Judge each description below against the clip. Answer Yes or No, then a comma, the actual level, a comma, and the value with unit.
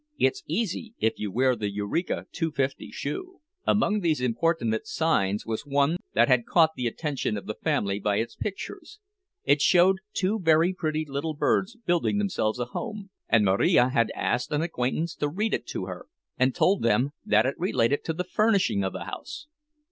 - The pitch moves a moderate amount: No, wide, 7.7 semitones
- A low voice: No, medium, 145 Hz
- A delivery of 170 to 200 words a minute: Yes, average, 185 wpm